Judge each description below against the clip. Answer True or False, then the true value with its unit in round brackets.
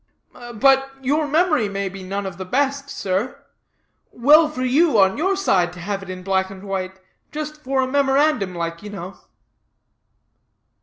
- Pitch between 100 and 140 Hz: False (215 Hz)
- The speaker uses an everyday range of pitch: False (6.9 semitones)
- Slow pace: False (165 wpm)